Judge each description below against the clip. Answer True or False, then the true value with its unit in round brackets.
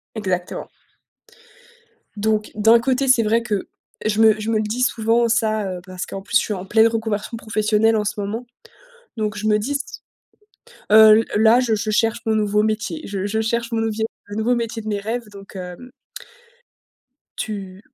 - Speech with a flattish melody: True (1.5 semitones)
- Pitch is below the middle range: False (220 Hz)